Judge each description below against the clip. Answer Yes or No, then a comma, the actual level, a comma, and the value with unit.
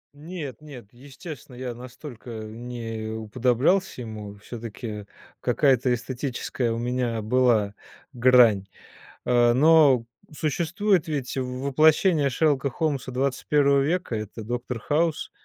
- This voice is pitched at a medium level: No, low, 125 Hz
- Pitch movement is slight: No, average, 3.7 semitones